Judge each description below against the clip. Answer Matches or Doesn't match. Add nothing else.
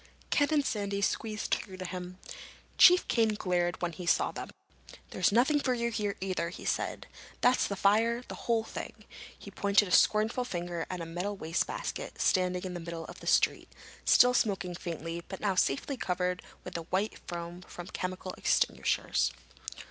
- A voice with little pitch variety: Doesn't match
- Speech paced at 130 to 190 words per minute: Matches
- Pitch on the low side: Doesn't match